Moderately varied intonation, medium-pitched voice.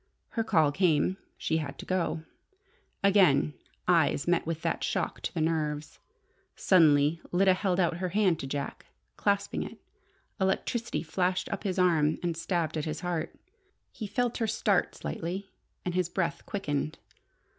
Yes: average, 3.3 semitones; medium, 175 Hz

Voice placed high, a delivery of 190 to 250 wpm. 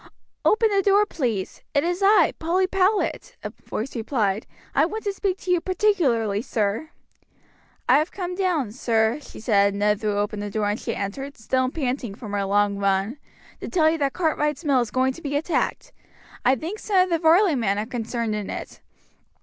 Yes: very high, 265 Hz; average, 200 wpm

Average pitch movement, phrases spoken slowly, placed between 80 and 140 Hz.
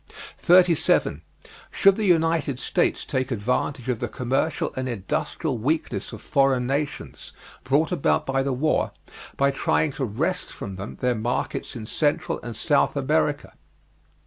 No: average, 4.1 semitones; average, 145 wpm; low, 135 Hz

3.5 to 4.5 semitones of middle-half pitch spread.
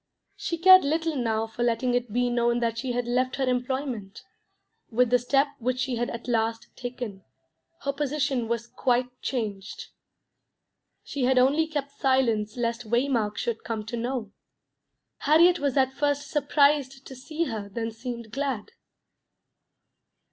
No: average, 3.0 semitones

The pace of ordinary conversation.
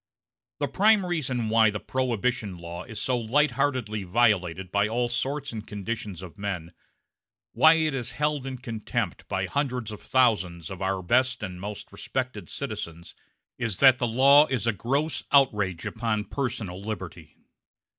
Yes: average, 155 wpm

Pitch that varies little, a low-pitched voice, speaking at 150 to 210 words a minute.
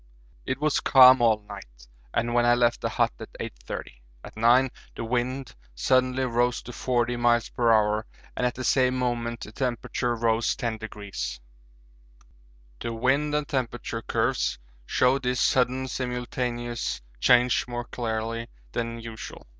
No: narrow, 1.6 semitones; low, 120 Hz; average, 140 wpm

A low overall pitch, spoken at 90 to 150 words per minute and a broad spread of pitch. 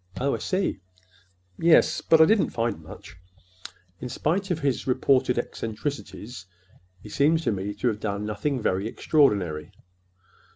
Yes: low, 125 Hz; average, 140 wpm; wide, 6.4 semitones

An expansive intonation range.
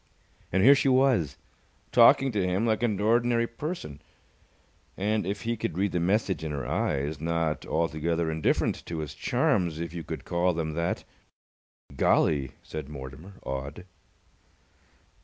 Yes: wide, 5.7 semitones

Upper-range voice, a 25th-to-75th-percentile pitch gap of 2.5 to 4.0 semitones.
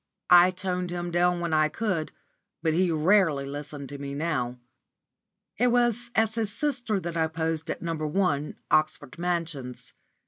No: medium, 170 Hz; average, 3.5 semitones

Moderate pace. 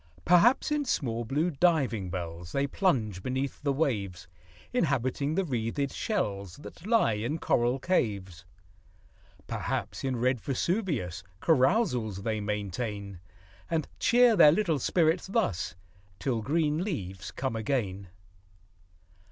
No: slow, 120 wpm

